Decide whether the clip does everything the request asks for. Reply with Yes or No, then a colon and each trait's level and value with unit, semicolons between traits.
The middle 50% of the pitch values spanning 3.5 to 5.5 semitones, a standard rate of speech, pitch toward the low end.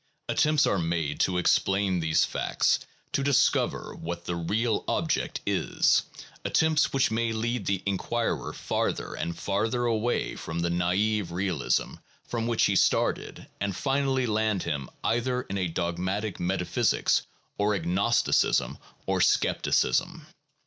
No: average, 5.1 semitones; slow, 130 wpm; low, 100 Hz